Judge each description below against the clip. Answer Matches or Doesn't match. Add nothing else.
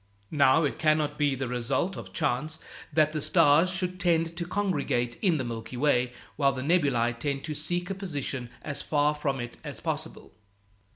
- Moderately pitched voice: Matches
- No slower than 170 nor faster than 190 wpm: Matches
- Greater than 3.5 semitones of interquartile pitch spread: Matches